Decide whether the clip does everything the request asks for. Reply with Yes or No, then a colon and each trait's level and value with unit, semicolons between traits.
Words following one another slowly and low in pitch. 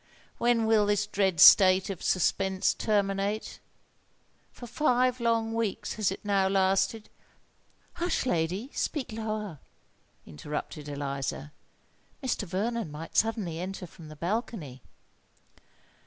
No: slow, 110 wpm; high, 195 Hz